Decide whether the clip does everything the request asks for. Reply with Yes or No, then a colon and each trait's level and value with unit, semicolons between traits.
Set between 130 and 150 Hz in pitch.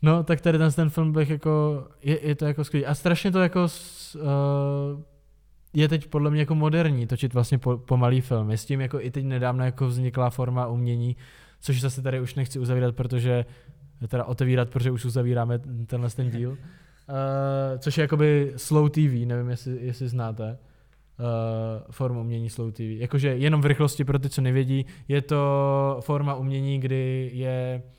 Yes: low, 135 Hz